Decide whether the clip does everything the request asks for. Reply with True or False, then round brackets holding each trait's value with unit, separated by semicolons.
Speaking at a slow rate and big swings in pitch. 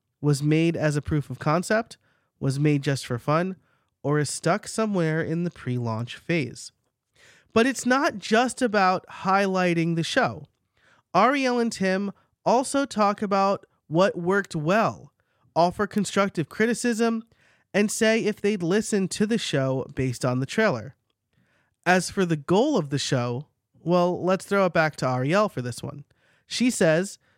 False (155 wpm; 6.6 semitones)